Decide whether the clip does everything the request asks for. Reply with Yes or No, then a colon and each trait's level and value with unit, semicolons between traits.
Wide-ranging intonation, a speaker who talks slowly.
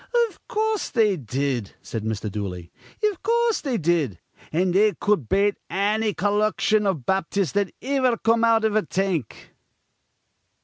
No: wide, 6.9 semitones; average, 145 wpm